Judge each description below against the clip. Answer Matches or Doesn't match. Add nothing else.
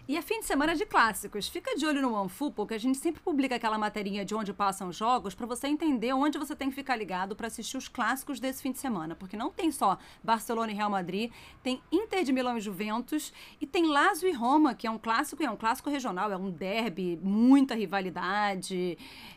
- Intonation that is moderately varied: Doesn't match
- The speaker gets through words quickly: Matches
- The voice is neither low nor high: Doesn't match